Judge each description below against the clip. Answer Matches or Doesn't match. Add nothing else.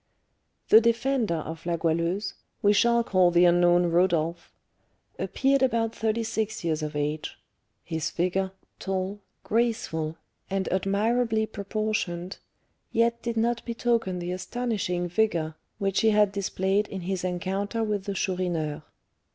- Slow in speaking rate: Matches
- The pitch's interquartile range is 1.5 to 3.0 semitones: Doesn't match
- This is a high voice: Matches